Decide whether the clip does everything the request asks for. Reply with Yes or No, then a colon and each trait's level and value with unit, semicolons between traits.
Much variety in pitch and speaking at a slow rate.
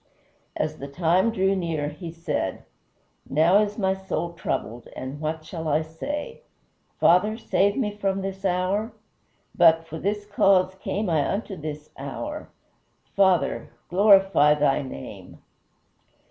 No: average, 4.1 semitones; slow, 130 wpm